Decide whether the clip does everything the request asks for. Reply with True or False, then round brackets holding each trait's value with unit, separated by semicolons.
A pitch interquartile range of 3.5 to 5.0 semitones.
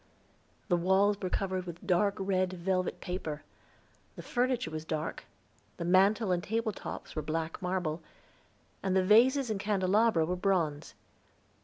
False (2.9 semitones)